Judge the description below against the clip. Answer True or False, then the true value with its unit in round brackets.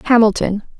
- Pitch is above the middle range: True (220 Hz)